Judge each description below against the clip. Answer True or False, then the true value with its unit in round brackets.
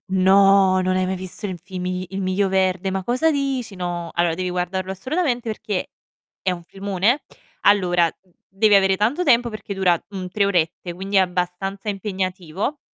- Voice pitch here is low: False (190 Hz)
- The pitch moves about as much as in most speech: False (2.0 semitones)